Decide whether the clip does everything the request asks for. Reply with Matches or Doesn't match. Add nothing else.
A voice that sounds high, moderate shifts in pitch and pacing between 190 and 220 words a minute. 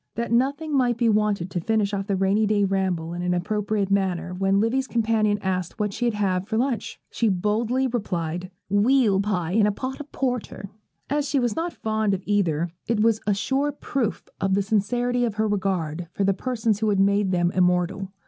Matches